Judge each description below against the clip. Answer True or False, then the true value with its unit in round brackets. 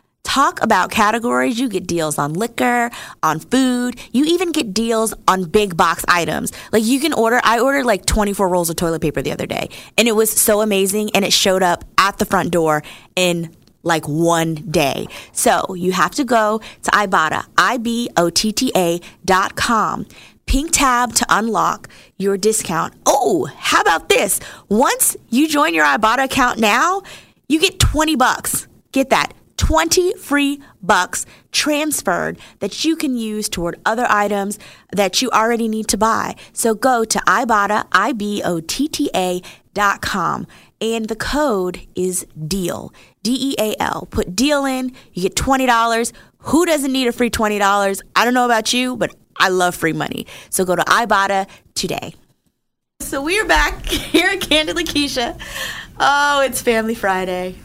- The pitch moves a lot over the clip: True (5.8 semitones)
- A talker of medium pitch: False (220 Hz)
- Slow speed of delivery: False (170 wpm)